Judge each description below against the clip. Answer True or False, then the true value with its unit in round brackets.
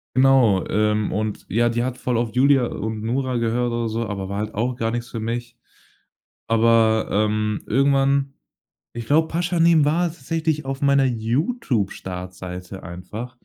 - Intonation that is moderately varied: True (4.0 semitones)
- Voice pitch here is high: False (120 Hz)